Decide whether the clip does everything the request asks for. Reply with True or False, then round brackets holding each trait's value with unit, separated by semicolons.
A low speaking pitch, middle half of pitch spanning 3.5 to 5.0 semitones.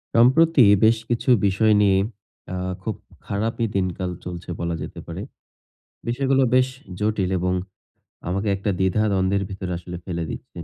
True (100 Hz; 3.9 semitones)